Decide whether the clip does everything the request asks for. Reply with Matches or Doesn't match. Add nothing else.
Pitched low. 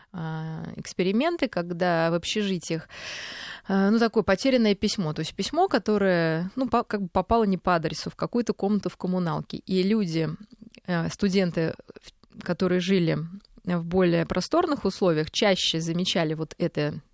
Doesn't match